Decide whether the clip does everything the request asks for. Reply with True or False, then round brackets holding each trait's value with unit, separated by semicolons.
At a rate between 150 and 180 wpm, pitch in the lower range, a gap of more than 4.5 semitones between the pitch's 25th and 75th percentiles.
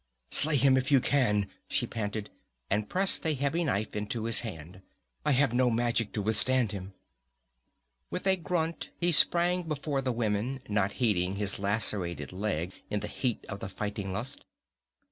True (165 wpm; 115 Hz; 5.4 semitones)